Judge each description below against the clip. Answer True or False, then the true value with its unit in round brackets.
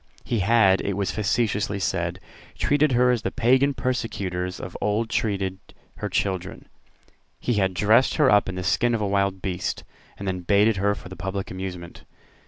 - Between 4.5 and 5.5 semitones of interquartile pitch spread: False (3.4 semitones)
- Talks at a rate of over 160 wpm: True (180 wpm)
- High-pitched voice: False (100 Hz)